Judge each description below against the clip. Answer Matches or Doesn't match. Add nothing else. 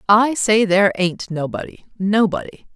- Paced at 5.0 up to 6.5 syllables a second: Doesn't match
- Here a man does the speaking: Doesn't match